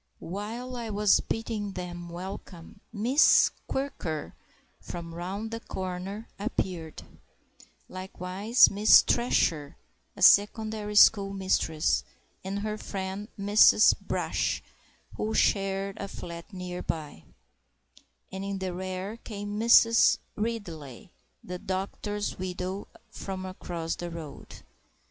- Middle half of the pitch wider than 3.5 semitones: No, average, 2.9 semitones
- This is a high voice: Yes, high, 195 Hz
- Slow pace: Yes, slow, 110 wpm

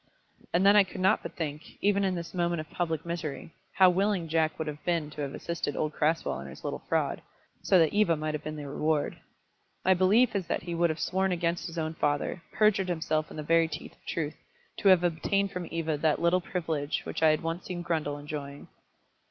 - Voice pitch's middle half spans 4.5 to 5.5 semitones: No, average, 2.9 semitones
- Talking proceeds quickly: Yes, fast, 225 wpm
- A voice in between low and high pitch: Yes, medium, 165 Hz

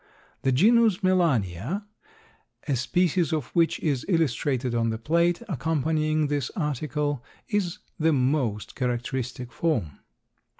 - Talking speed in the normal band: No, slow, 115 wpm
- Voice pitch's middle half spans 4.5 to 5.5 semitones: Yes, average, 5.2 semitones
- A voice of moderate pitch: Yes, medium, 150 Hz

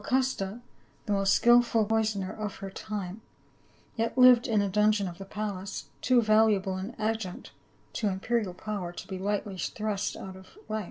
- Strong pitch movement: No, narrow, 2.5 semitones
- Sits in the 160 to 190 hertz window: No, high, 210 Hz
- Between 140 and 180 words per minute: Yes, average, 170 wpm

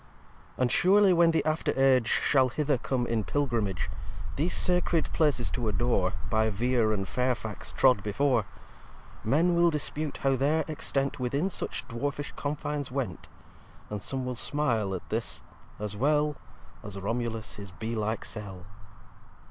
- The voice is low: Yes, low, 125 Hz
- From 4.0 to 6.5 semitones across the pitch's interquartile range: Yes, average, 5.2 semitones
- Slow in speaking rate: No, average, 150 wpm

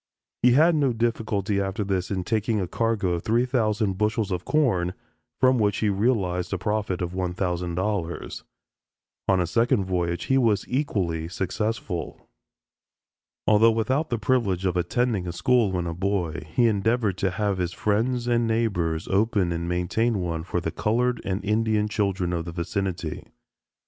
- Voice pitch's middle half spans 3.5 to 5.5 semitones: Yes, average, 4.2 semitones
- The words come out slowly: No, average, 160 wpm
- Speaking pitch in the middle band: No, low, 100 Hz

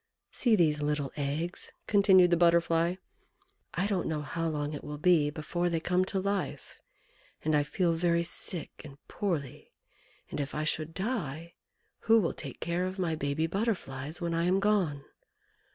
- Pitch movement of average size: Yes, average, 3.5 semitones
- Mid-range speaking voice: Yes, medium, 170 Hz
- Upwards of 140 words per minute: Yes, average, 170 wpm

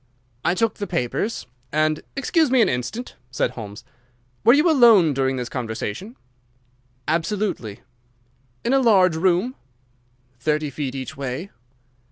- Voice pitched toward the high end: No, medium, 165 Hz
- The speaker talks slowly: Yes, slow, 130 wpm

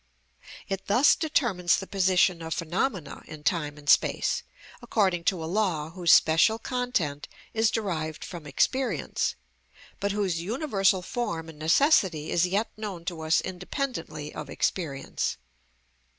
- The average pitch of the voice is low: No, medium, 180 Hz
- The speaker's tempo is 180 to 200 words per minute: No, slow, 135 wpm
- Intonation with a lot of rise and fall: No, average, 4.6 semitones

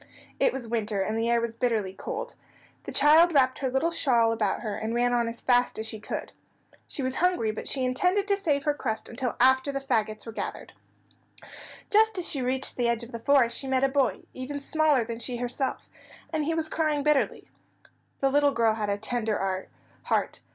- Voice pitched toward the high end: Yes, very high, 255 Hz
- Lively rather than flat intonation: No, average, 4.0 semitones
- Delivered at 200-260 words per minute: Yes, fast, 205 wpm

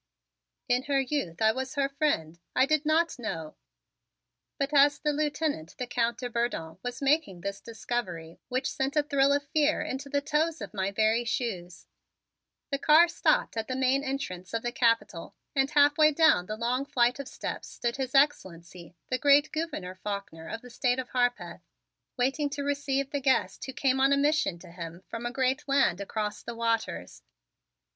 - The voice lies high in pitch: Yes, very high, 255 Hz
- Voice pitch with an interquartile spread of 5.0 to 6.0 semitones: No, average, 4.6 semitones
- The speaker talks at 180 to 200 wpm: Yes, average, 185 wpm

